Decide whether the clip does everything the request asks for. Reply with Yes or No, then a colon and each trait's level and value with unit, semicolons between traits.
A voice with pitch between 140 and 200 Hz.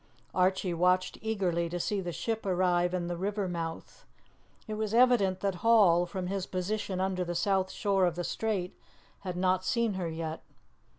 Yes: medium, 185 Hz